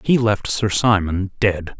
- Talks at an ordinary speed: Yes, average, 165 wpm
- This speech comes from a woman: No, male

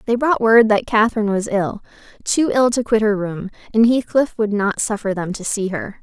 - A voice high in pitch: Yes, high, 220 Hz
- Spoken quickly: Yes, fast, 220 wpm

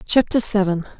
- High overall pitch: Yes, high, 205 Hz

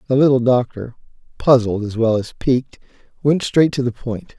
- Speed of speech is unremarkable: Yes, average, 180 wpm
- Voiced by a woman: No, male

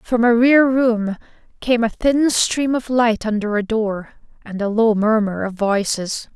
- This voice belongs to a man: No, female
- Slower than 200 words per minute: Yes, average, 180 wpm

